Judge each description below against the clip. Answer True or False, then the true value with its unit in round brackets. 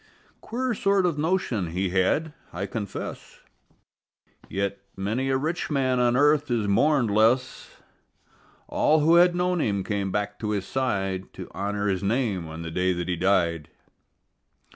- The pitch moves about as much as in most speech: False (7.3 semitones)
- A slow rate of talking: False (155 wpm)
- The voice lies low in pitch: True (110 Hz)